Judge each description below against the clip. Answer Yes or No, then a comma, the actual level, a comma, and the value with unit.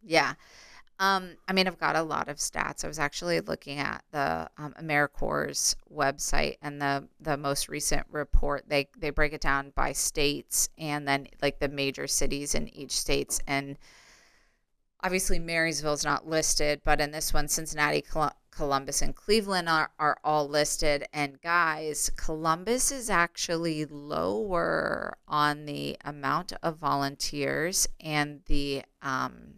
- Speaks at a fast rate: No, average, 150 wpm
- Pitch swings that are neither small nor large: No, narrow, 2.2 semitones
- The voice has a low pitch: No, medium, 150 Hz